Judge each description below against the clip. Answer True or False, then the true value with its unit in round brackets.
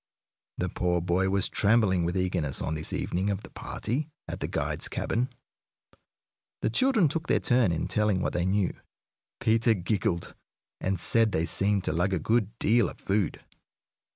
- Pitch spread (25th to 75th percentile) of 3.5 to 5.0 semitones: True (4.1 semitones)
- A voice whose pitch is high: False (100 Hz)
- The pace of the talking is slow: False (170 wpm)